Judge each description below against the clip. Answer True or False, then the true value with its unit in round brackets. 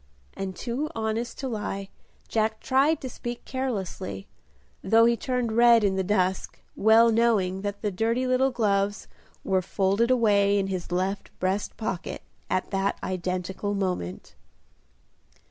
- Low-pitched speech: False (205 Hz)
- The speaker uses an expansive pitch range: False (3.6 semitones)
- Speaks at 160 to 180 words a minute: False (140 wpm)